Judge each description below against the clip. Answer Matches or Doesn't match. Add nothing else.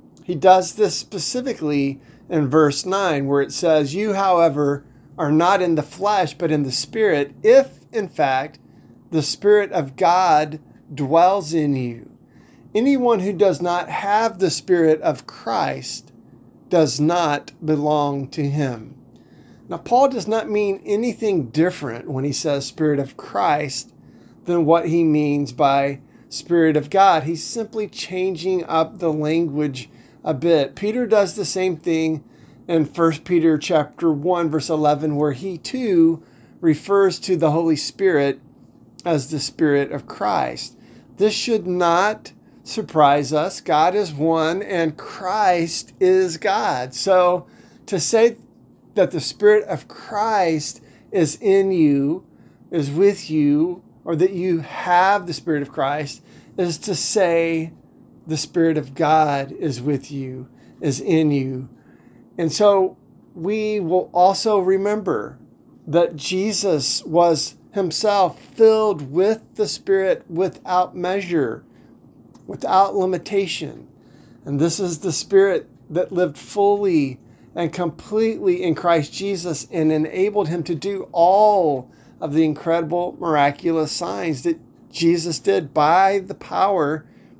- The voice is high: Doesn't match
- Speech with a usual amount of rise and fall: Matches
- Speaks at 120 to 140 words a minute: Matches